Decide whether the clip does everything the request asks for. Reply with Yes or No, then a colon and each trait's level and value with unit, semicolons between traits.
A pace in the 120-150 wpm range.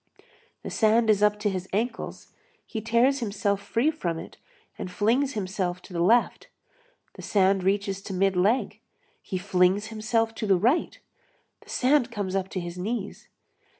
No: average, 165 wpm